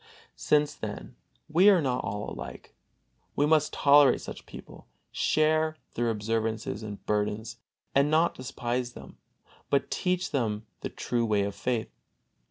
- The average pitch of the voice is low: Yes, low, 120 Hz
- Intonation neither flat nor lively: No, wide, 6.0 semitones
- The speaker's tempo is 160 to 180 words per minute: No, average, 140 wpm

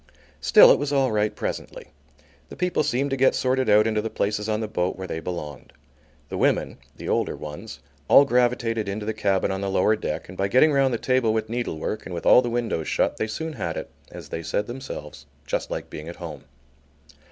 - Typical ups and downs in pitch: Yes, average, 4.7 semitones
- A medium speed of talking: No, fast, 220 wpm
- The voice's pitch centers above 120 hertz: No, low, 110 Hz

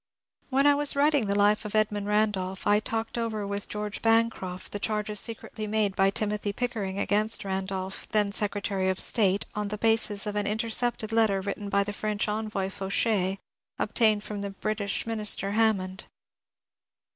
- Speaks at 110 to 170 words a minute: Yes, average, 165 wpm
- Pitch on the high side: Yes, high, 210 Hz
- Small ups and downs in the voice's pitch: Yes, narrow, 1.7 semitones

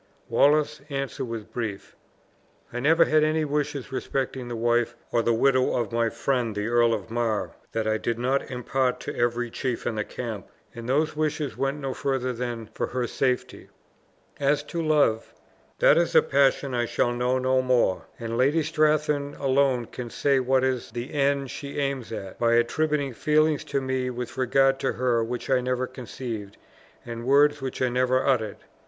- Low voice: Yes, low, 130 Hz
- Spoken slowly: No, average, 180 wpm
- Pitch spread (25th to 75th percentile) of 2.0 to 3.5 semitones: Yes, average, 2.8 semitones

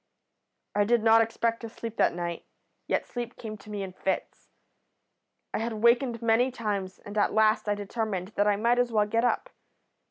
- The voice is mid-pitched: No, high, 220 Hz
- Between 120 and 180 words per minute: No, average, 190 wpm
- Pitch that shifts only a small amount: Yes, narrow, 2.2 semitones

